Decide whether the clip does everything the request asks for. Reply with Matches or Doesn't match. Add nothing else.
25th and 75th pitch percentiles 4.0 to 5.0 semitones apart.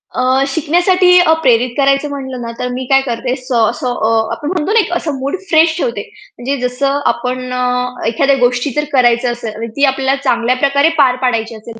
Doesn't match